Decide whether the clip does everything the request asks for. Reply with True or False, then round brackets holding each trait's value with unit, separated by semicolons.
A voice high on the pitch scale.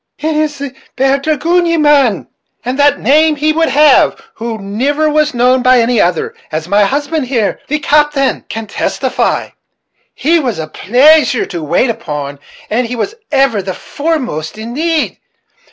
True (270 Hz)